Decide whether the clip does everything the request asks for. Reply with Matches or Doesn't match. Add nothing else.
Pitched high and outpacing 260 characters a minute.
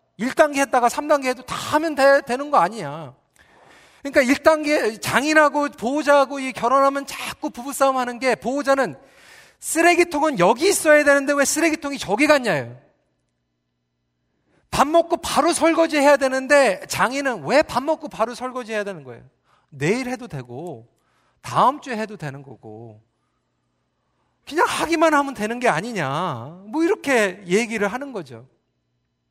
Matches